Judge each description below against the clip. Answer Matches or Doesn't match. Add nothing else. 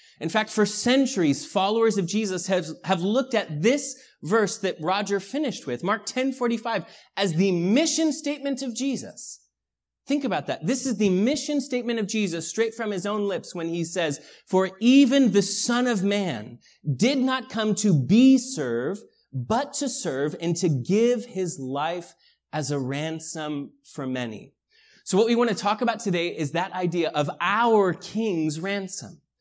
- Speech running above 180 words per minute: Doesn't match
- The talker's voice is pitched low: Doesn't match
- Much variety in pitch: Matches